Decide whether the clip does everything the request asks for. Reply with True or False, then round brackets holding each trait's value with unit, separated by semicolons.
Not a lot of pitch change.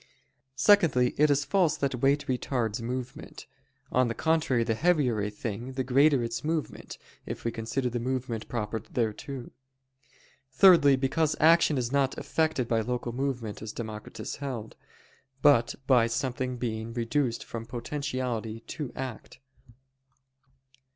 False (3.4 semitones)